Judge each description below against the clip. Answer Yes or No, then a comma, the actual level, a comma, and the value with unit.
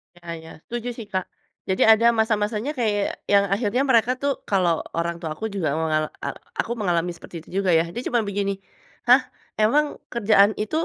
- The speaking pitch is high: Yes, high, 205 Hz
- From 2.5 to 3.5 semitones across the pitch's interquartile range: No, average, 4.3 semitones